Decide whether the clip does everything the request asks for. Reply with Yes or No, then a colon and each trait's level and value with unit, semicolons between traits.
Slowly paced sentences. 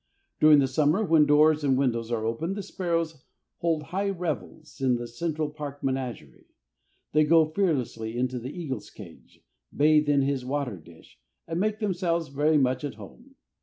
No: average, 165 wpm